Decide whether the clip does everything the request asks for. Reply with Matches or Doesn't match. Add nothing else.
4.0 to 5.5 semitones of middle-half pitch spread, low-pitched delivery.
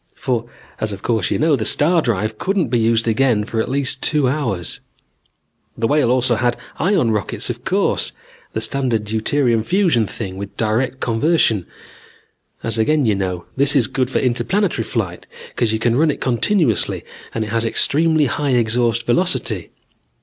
Matches